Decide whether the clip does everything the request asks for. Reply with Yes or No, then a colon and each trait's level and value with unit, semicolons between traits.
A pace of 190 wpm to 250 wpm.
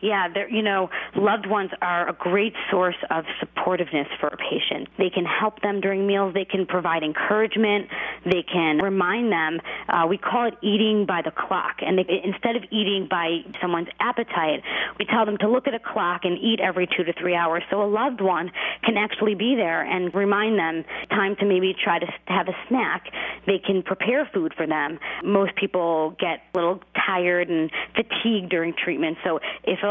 Yes: average, 195 wpm